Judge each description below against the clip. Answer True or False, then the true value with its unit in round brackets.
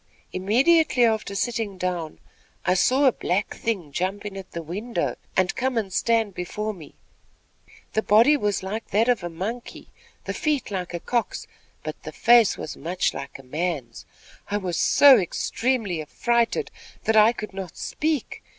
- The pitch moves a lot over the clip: False (4.6 semitones)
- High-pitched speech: True (210 Hz)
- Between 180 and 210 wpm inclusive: False (165 wpm)